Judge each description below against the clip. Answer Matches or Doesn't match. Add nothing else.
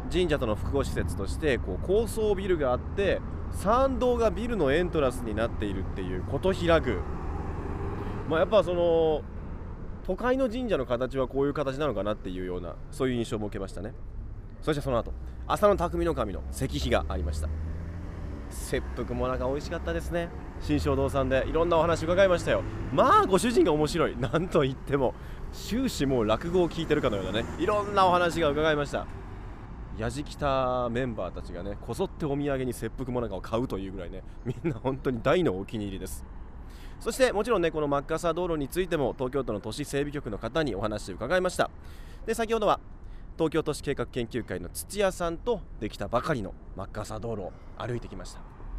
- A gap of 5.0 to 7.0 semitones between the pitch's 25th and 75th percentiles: Doesn't match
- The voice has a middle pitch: Doesn't match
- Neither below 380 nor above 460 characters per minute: Matches